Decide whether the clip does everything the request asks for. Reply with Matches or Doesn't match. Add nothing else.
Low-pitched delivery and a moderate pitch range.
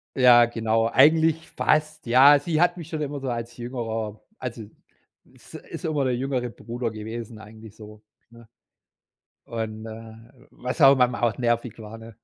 Matches